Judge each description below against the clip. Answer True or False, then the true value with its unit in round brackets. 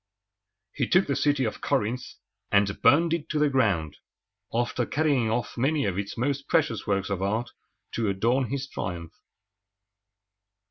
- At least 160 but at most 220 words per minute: False (150 wpm)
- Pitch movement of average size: False (5.8 semitones)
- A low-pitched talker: True (120 Hz)